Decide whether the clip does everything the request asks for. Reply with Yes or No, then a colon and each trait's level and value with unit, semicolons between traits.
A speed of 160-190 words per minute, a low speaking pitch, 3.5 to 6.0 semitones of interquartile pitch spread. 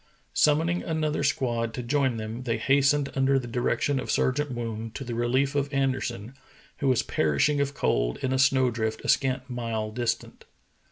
No: average, 175 wpm; low, 130 Hz; average, 3.1 semitones